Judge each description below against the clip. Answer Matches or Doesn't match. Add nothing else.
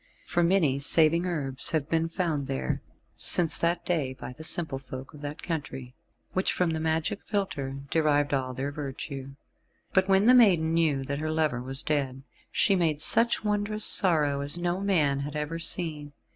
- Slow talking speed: Doesn't match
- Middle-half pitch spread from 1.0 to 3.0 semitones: Doesn't match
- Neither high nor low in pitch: Matches